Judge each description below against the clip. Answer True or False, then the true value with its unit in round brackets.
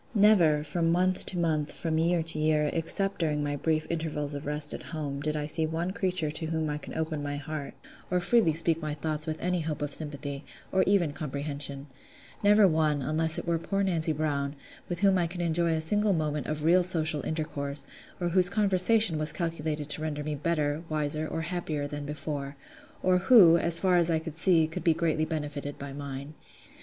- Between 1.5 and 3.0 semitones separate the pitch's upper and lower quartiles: True (2.5 semitones)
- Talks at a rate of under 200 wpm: False (205 wpm)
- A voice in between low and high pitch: True (155 Hz)